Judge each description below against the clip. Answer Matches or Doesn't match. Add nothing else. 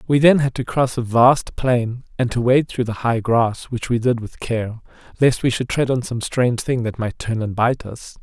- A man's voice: Matches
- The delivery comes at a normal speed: Doesn't match